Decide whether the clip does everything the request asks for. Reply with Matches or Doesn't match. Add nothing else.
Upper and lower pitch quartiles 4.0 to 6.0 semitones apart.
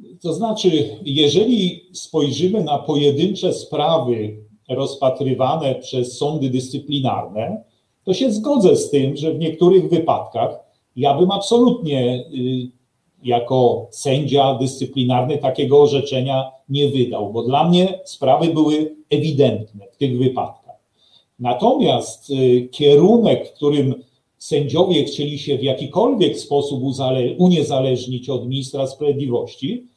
Doesn't match